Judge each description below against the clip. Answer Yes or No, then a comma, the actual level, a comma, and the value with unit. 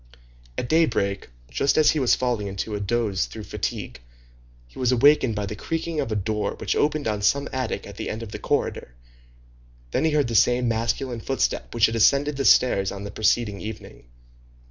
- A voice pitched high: No, low, 115 Hz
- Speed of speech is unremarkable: Yes, average, 195 wpm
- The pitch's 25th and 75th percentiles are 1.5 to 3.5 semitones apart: No, average, 4.8 semitones